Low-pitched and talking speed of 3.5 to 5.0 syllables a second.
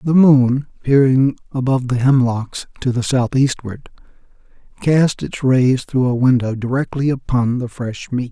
Yes: low, 130 Hz; 4.4 syllables/s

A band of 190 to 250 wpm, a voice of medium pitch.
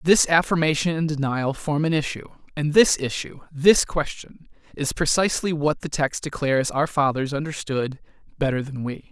No: average, 150 wpm; medium, 150 Hz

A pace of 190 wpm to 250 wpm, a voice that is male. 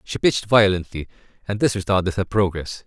No: average, 165 wpm; male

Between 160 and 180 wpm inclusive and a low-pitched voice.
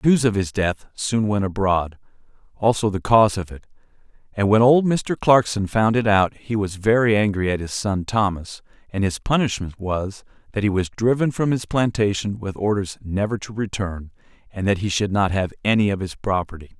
No: average, 195 wpm; low, 105 Hz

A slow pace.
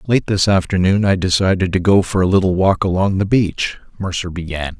No: average, 200 wpm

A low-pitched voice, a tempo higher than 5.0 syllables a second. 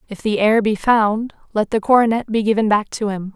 No: high, 215 Hz; 5.4 syllables/s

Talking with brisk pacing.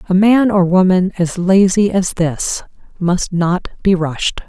No: average, 160 wpm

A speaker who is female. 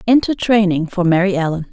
Yes: female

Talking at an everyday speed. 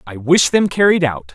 No: fast, 225 wpm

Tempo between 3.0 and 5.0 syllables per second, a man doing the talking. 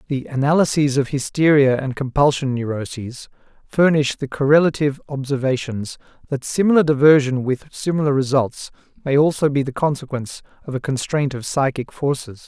No: 5.4 syllables/s; male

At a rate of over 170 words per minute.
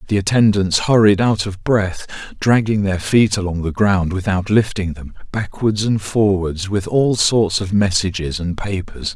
No: average, 165 wpm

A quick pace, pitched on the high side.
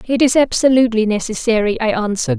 No: average, 150 wpm; high, 220 Hz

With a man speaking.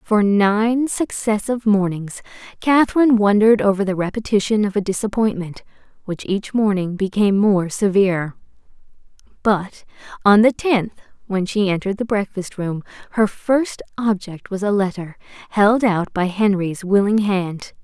No: female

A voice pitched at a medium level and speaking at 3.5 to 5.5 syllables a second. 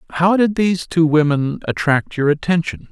Yes: medium, 165 Hz; 5.2 syllables/s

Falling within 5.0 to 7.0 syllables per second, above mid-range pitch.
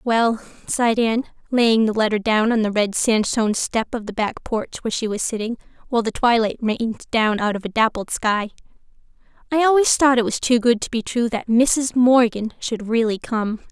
Yes: 5.2 syllables/s; high, 230 Hz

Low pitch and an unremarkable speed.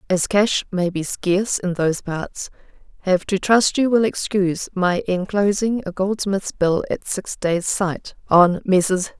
No: high, 190 Hz; average, 165 wpm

